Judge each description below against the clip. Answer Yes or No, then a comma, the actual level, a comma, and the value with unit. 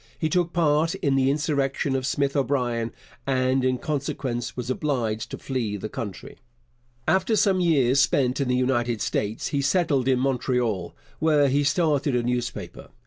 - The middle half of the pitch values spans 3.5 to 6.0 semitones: No, average, 2.9 semitones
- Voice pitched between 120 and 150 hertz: Yes, low, 135 Hz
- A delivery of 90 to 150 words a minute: No, average, 160 wpm